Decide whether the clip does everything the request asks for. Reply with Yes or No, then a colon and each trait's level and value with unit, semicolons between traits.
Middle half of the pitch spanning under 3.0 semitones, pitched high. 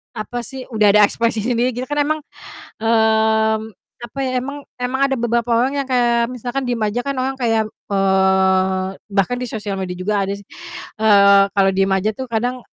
No: average, 3.8 semitones; high, 225 Hz